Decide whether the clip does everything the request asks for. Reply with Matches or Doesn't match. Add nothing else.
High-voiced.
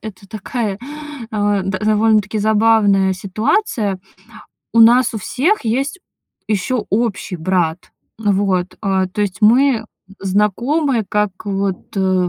Matches